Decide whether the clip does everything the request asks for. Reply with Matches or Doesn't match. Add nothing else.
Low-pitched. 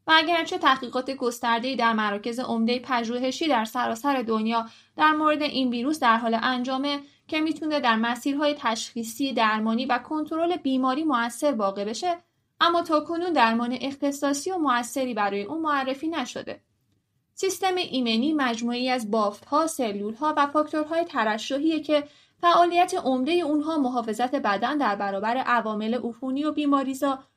Doesn't match